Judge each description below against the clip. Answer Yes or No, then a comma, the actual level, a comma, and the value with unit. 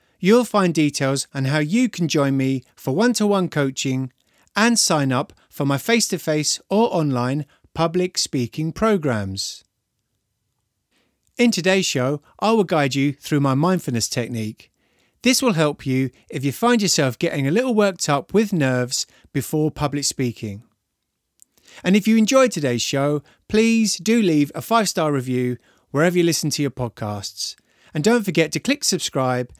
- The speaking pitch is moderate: Yes, medium, 150 Hz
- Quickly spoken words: No, average, 165 wpm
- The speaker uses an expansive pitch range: Yes, wide, 6.7 semitones